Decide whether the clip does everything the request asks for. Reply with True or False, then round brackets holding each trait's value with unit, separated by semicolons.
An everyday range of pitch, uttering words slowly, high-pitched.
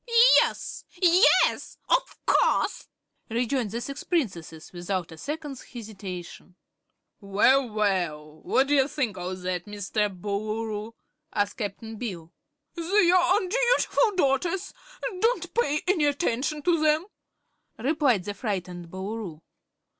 False (8.0 semitones; 115 wpm; 225 Hz)